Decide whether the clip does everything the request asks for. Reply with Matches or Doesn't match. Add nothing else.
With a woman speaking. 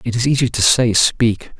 Doesn't match